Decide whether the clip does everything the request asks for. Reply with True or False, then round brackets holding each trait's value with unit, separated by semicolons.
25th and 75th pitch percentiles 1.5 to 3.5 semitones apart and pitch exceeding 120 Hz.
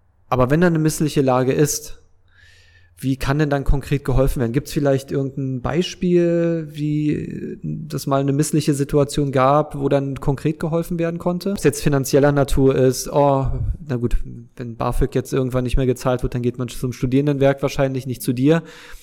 True (2.8 semitones; 140 Hz)